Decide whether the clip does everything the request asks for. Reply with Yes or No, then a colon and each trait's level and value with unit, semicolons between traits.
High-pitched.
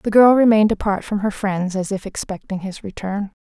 Yes: high, 200 Hz